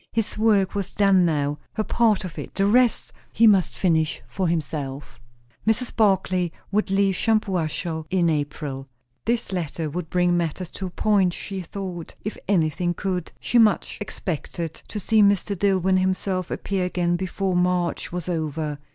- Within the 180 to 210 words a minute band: No, average, 160 wpm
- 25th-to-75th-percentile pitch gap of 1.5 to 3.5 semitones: Yes, average, 3.2 semitones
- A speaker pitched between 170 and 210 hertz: Yes, medium, 185 Hz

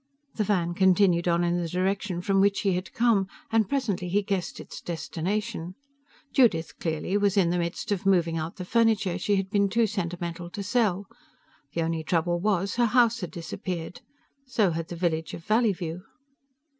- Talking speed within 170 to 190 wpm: Yes, average, 180 wpm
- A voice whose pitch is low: No, medium, 185 Hz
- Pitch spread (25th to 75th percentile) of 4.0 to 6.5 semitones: No, average, 3.1 semitones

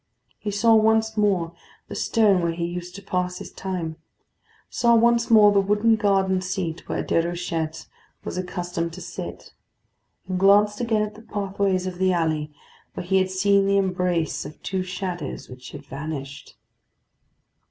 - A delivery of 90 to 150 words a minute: No, average, 160 wpm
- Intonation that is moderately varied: Yes, average, 3.1 semitones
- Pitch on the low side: No, medium, 185 Hz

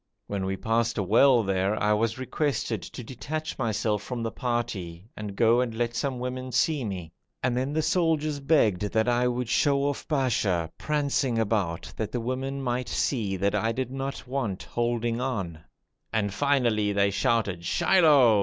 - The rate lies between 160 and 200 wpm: Yes, average, 175 wpm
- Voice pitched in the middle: No, low, 120 Hz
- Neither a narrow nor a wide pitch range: Yes, average, 4.3 semitones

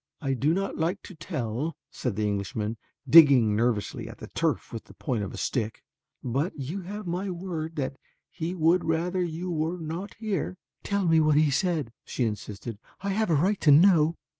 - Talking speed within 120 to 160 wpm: No, average, 190 wpm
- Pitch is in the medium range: Yes, medium, 160 Hz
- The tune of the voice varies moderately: No, wide, 6.0 semitones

